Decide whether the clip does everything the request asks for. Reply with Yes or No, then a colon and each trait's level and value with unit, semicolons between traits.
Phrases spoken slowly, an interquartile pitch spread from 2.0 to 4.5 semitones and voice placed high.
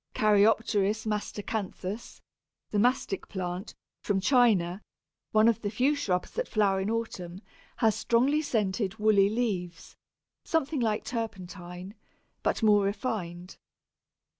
Yes: slow, 115 wpm; average, 3.1 semitones; high, 210 Hz